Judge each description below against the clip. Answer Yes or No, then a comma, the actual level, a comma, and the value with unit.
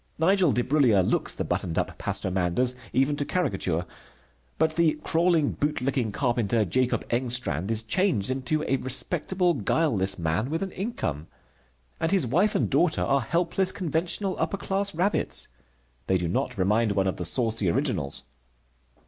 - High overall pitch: No, low, 130 Hz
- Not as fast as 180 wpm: Yes, average, 150 wpm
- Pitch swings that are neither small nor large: No, wide, 8.6 semitones